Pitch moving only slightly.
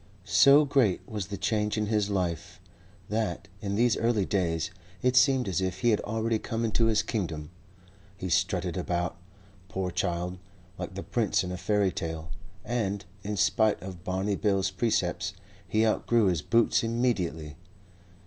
No: average, 3.7 semitones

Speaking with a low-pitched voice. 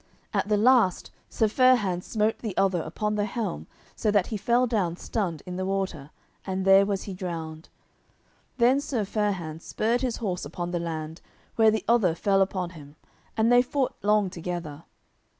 No: high, 195 Hz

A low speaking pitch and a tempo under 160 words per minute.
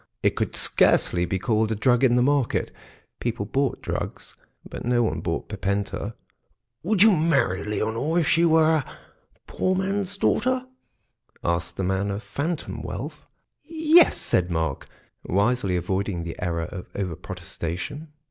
Yes: low, 115 Hz; average, 145 wpm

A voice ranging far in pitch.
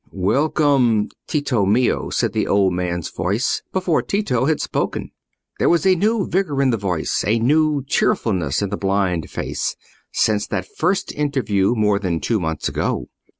Yes: wide, 7.2 semitones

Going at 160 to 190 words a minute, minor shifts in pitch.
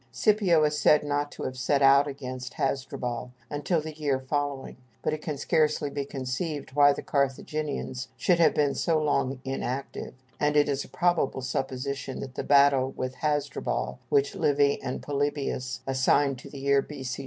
Yes: average, 170 wpm; narrow, 2.1 semitones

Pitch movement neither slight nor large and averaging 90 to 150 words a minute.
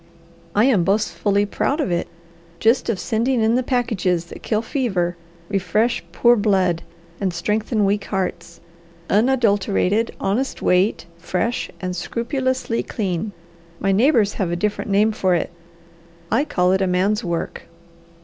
Yes: average, 4.0 semitones; average, 140 wpm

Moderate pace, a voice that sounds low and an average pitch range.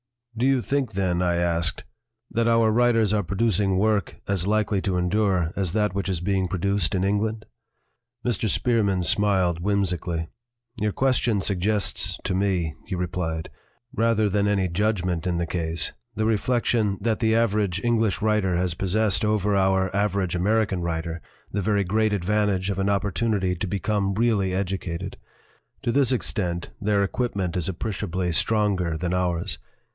Yes: average, 155 wpm; low, 100 Hz; average, 3.0 semitones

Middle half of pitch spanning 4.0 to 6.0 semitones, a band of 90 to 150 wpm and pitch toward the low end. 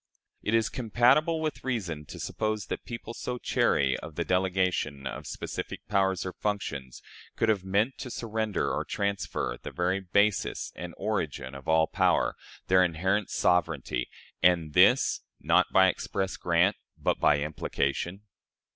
Yes: average, 4.6 semitones; average, 145 wpm; very low, 95 Hz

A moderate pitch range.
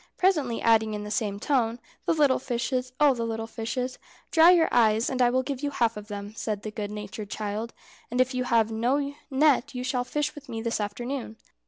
Yes: average, 3.2 semitones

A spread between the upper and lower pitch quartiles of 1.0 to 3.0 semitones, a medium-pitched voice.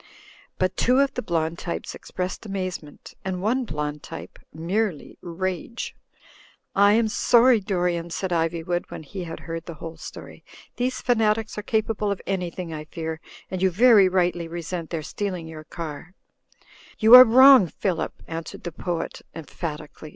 No: average, 4.3 semitones; medium, 180 Hz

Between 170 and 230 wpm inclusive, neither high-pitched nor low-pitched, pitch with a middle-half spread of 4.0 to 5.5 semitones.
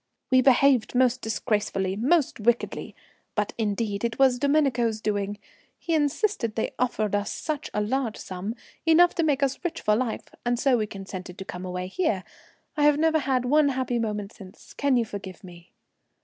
No: average, 175 wpm; high, 235 Hz; average, 5.1 semitones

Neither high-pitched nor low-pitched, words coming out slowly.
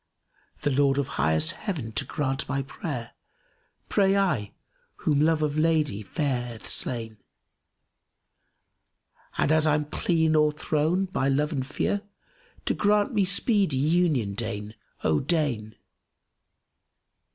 Yes: medium, 145 Hz; slow, 130 wpm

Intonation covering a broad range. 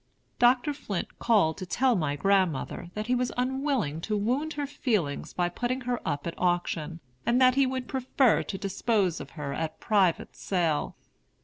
Yes: wide, 7.0 semitones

